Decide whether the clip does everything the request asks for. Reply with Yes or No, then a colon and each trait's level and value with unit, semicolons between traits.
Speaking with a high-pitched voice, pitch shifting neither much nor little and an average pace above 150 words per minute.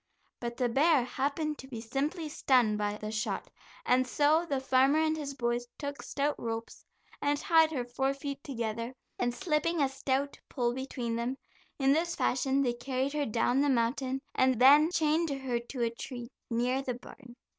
Yes: very high, 265 Hz; average, 3.1 semitones; average, 180 wpm